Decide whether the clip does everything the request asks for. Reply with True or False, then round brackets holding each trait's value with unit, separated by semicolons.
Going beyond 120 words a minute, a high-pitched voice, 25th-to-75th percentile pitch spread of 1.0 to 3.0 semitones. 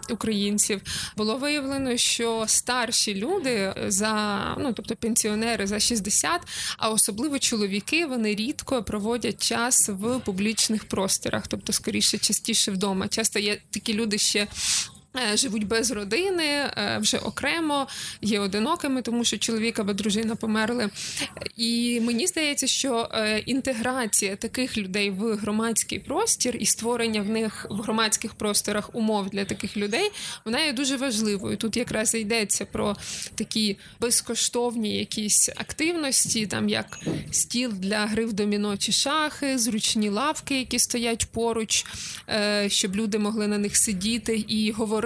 True (130 wpm; 225 Hz; 2.5 semitones)